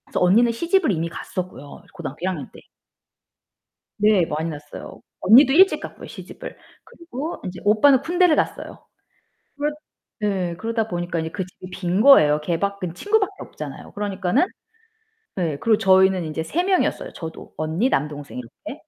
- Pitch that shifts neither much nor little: No, wide, 7.0 semitones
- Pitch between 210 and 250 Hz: No, high, 190 Hz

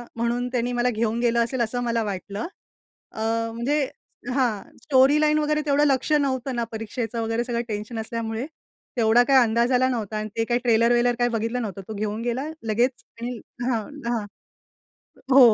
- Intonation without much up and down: Yes, narrow, 2.1 semitones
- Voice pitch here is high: Yes, high, 235 Hz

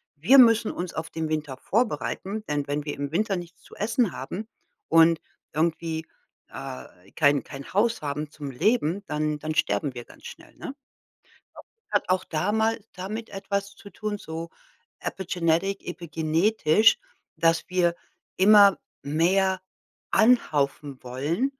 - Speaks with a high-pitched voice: No, medium, 170 Hz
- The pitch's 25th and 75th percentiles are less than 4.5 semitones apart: No, average, 5.0 semitones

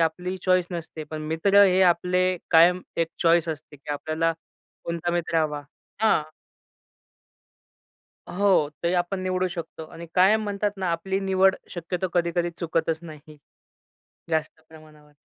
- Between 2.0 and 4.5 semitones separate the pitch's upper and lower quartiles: Yes, narrow, 2.4 semitones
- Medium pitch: Yes, medium, 170 Hz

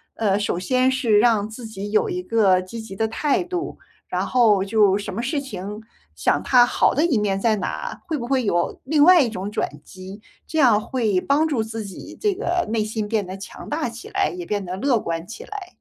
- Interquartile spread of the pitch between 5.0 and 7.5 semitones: Yes, wide, 5.5 semitones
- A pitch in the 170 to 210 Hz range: No, high, 225 Hz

